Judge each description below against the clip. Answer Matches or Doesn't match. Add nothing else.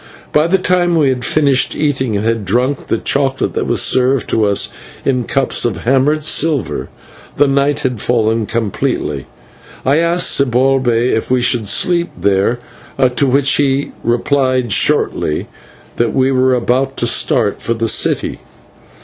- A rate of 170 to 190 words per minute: Doesn't match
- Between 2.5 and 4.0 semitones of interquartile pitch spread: Matches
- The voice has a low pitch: Matches